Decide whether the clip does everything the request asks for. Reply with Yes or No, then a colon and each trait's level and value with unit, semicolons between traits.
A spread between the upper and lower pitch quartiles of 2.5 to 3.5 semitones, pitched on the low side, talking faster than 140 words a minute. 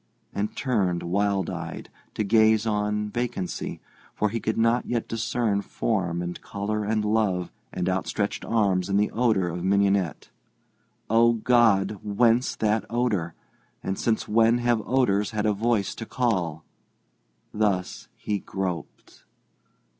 No: average, 2.8 semitones; low, 105 Hz; slow, 135 wpm